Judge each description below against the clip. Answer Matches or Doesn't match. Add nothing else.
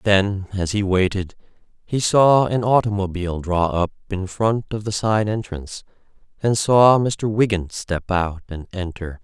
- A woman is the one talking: Doesn't match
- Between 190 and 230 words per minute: Doesn't match